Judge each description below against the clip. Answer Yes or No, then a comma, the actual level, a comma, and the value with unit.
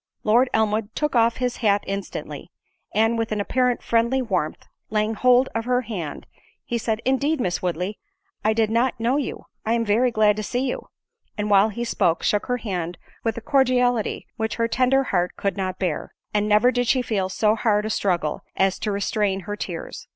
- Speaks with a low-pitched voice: No, high, 220 Hz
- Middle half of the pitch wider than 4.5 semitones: No, average, 3.4 semitones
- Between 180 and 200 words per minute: Yes, average, 190 wpm